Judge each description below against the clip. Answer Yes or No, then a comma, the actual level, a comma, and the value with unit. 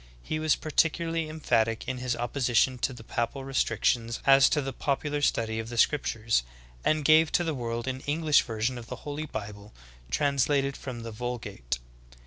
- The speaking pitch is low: Yes, low, 130 Hz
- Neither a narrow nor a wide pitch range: Yes, average, 4.2 semitones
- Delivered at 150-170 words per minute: No, average, 180 wpm